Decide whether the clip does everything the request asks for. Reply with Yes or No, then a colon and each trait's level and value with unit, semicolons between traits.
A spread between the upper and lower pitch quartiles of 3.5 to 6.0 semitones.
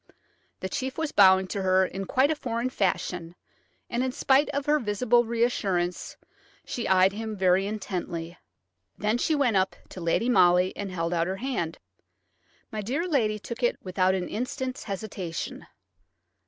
Yes: average, 5.1 semitones